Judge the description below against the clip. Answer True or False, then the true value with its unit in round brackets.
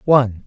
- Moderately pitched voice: False (125 Hz)